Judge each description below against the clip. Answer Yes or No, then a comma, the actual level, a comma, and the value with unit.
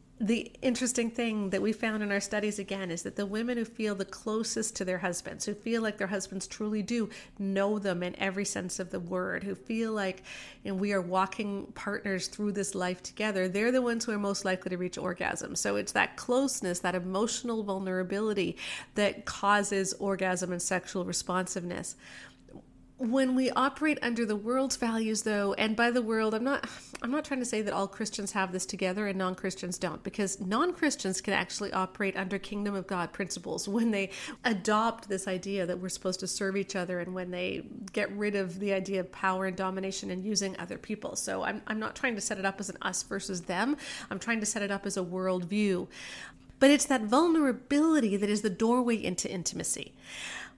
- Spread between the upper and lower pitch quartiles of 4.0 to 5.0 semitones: No, average, 3.0 semitones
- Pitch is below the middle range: No, high, 200 Hz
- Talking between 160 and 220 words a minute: Yes, average, 200 wpm